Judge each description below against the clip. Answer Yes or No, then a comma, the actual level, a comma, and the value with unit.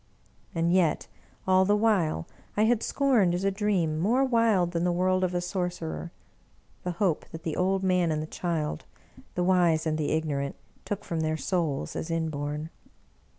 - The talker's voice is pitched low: No, medium, 175 Hz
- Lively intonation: No, average, 3.2 semitones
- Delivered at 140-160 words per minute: No, average, 175 wpm